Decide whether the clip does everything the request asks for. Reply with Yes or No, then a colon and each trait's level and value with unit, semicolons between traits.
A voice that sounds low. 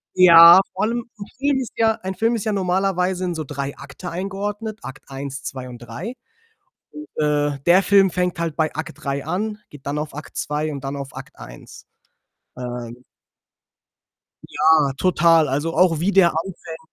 No: medium, 165 Hz